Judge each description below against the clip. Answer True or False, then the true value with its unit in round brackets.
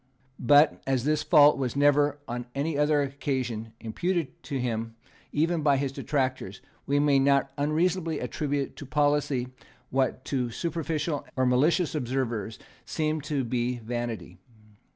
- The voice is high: False (140 Hz)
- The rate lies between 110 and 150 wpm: True (135 wpm)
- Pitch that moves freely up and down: False (3.0 semitones)